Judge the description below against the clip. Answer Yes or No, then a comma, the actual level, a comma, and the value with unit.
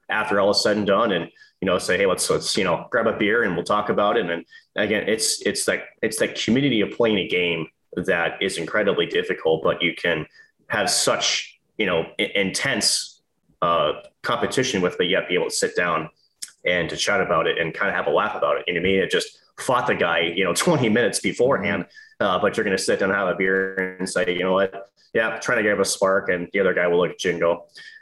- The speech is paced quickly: Yes, fast, 245 wpm